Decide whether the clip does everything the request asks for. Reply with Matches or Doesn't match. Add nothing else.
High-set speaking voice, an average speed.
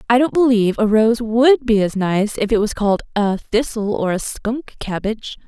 Doesn't match